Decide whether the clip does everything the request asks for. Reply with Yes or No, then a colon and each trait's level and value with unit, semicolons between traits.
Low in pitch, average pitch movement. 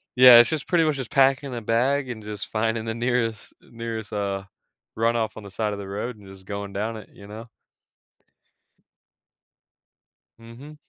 Yes: low, 115 Hz; average, 3.1 semitones